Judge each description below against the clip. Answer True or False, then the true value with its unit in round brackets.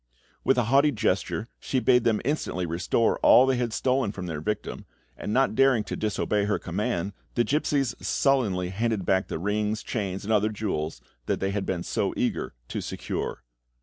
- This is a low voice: True (105 Hz)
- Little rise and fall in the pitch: False (4.5 semitones)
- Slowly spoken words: False (180 wpm)